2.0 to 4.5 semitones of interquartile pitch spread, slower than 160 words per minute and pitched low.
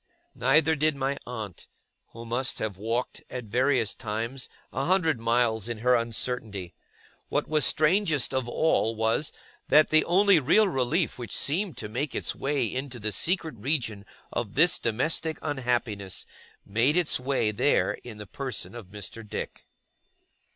No: average, 5.0 semitones; average, 150 wpm; low, 125 Hz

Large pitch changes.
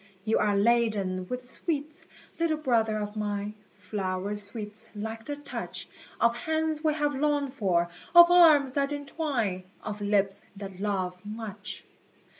Yes: wide, 6.0 semitones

